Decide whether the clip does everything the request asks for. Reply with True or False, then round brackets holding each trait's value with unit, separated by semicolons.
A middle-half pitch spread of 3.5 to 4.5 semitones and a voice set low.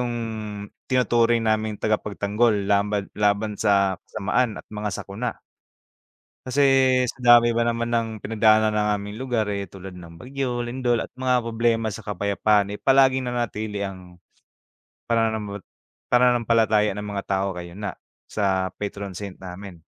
False (2.8 semitones; 105 Hz)